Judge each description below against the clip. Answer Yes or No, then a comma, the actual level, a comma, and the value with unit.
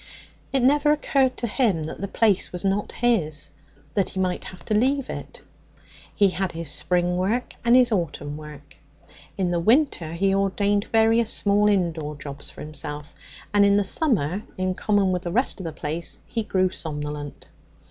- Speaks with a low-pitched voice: No, high, 190 Hz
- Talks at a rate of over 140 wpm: Yes, average, 180 wpm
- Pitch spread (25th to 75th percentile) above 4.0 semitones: Yes, average, 5.3 semitones